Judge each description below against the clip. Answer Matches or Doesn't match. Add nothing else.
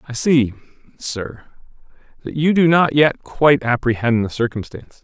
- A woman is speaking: Doesn't match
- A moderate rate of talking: Matches